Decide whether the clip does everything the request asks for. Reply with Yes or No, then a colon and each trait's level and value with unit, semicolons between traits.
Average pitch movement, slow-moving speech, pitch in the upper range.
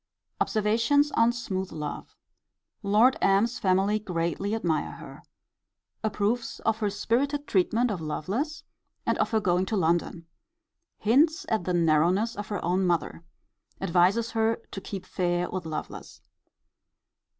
Yes: average, 4.3 semitones; slow, 130 wpm; high, 200 Hz